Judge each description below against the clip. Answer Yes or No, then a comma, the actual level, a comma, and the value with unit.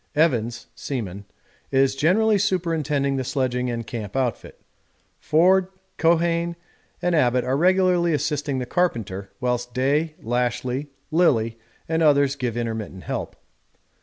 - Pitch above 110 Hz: Yes, low, 135 Hz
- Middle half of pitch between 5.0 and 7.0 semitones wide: Yes, average, 5.3 semitones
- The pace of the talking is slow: Yes, slow, 120 wpm